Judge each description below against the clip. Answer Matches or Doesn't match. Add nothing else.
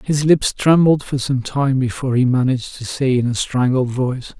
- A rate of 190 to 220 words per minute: Matches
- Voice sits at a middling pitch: Doesn't match